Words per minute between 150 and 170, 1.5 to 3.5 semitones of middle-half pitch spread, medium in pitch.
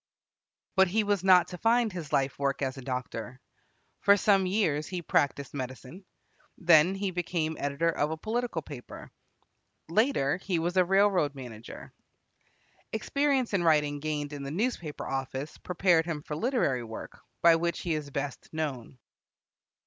No: average, 155 wpm; average, 5.2 semitones; medium, 160 Hz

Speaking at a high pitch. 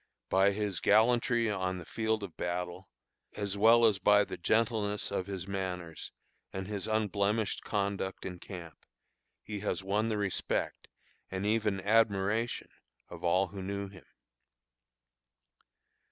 No: low, 100 Hz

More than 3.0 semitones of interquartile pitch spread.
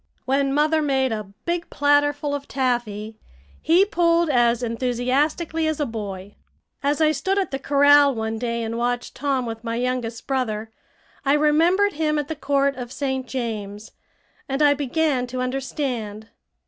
Yes: average, 4.0 semitones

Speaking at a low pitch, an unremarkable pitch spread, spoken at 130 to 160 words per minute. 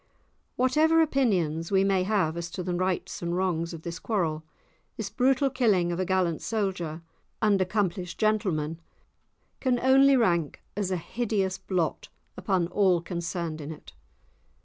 No: medium, 185 Hz; average, 4.1 semitones; average, 150 wpm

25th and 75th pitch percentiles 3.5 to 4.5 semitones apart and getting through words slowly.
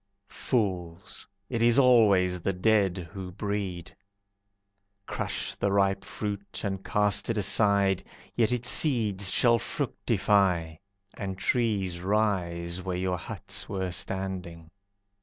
No: narrow, 2.5 semitones; slow, 115 wpm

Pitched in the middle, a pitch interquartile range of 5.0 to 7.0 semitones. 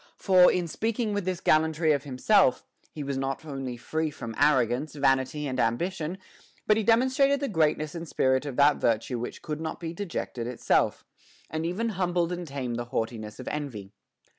Yes: medium, 150 Hz; average, 5.3 semitones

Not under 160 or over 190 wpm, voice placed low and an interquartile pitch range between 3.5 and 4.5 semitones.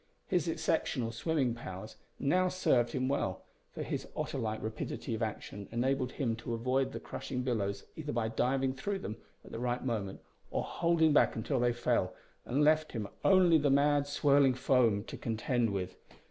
Yes: average, 175 wpm; low, 125 Hz; average, 4.0 semitones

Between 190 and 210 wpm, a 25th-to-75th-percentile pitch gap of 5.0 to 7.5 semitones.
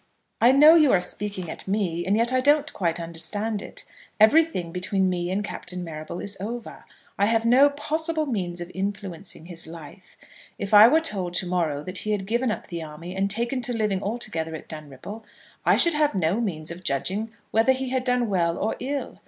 Yes: average, 200 wpm; wide, 5.5 semitones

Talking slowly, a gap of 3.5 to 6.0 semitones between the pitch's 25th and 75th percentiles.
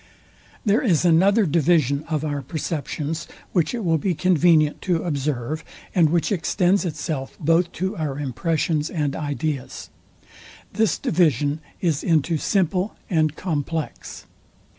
No: slow, 125 wpm; average, 3.1 semitones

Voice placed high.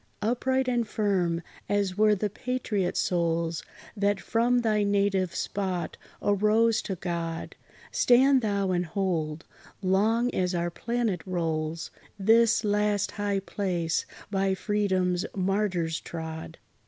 Yes: high, 195 Hz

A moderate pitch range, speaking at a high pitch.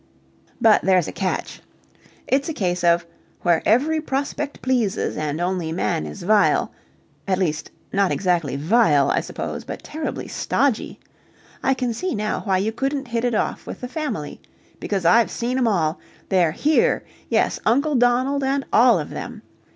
No: wide, 7.0 semitones; high, 220 Hz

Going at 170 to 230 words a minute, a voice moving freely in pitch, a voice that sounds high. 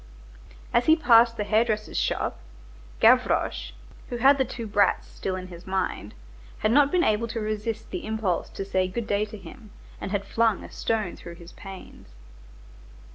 No: average, 180 wpm; average, 3.3 semitones; high, 215 Hz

